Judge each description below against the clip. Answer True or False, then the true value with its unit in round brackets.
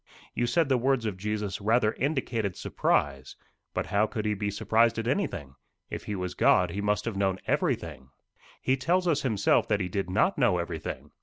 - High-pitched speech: False (105 Hz)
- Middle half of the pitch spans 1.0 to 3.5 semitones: False (4.4 semitones)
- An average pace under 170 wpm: False (195 wpm)